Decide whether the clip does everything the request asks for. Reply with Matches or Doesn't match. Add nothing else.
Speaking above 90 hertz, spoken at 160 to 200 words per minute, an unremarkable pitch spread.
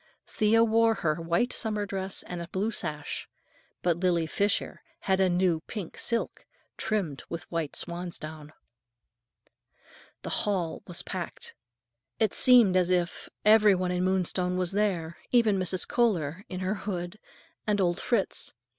Doesn't match